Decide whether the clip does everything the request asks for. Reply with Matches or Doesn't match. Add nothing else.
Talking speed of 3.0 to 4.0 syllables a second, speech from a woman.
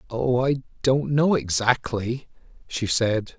Doesn't match